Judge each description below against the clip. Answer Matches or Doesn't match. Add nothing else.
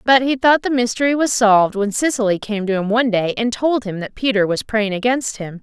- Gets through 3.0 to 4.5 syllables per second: Doesn't match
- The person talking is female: Matches